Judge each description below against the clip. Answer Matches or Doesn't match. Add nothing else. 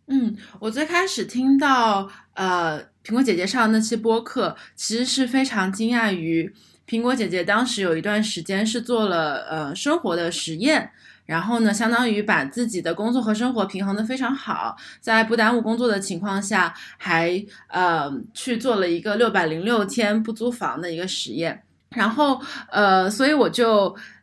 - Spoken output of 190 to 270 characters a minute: Matches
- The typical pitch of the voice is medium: Doesn't match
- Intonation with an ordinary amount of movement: Matches